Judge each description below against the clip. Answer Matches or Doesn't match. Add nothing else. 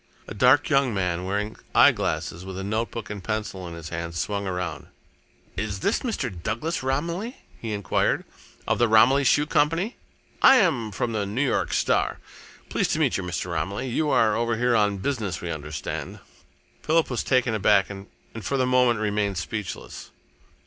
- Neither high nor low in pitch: Doesn't match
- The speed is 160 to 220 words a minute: Matches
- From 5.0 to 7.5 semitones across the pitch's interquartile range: Matches